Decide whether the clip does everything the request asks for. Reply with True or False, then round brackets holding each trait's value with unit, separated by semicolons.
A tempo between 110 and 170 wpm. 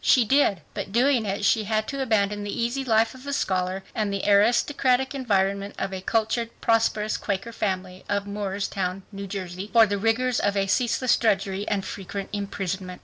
False (180 wpm)